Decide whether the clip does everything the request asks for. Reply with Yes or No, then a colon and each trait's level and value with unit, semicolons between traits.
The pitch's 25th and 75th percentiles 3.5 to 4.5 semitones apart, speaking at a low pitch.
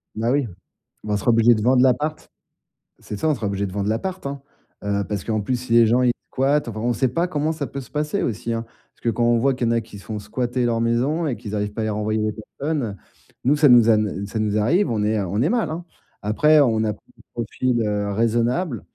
Yes: average, 4.2 semitones; low, 115 Hz